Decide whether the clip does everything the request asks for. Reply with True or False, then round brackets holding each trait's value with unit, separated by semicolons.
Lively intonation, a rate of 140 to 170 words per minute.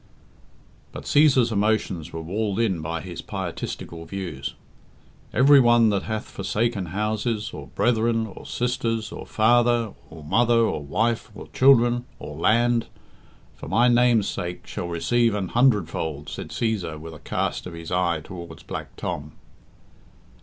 True (5.7 semitones; 145 wpm)